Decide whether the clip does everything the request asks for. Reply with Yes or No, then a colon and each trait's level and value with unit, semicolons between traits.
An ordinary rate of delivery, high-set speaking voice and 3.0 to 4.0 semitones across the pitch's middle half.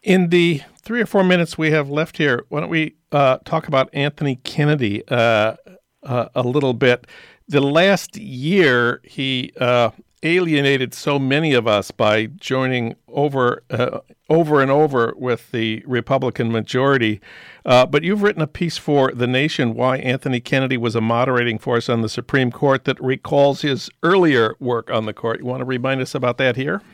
No: average, 180 wpm; low, 130 Hz; average, 3.6 semitones